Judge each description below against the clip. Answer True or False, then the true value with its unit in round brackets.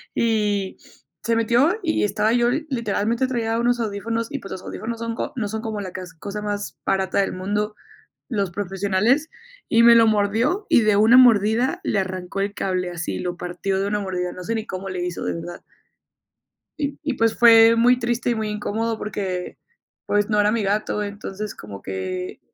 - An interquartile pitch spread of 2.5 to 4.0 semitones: True (3.1 semitones)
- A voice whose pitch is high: True (210 Hz)